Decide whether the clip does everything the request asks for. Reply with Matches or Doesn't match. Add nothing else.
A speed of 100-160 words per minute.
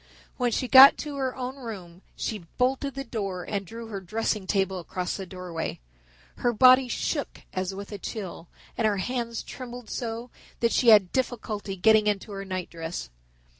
Doesn't match